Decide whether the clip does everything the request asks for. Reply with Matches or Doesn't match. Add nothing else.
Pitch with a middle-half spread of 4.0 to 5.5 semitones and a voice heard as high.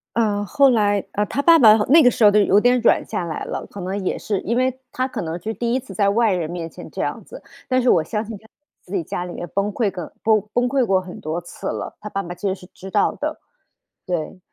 Matches